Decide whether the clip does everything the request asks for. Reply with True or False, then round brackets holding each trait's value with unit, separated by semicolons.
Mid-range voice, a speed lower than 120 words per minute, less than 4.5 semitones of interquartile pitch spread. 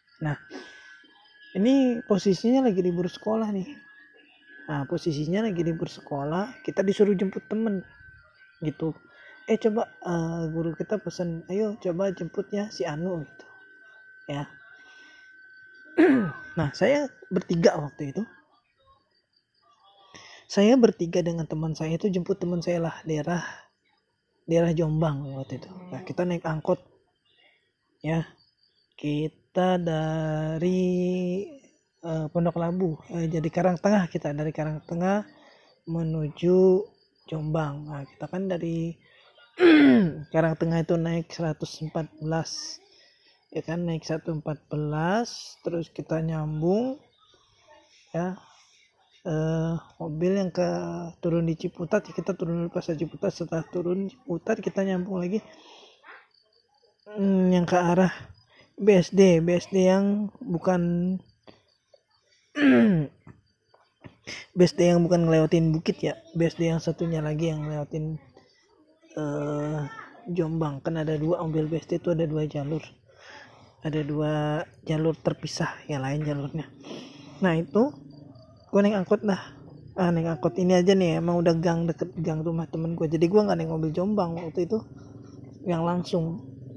False (170 Hz; 125 wpm; 3.6 semitones)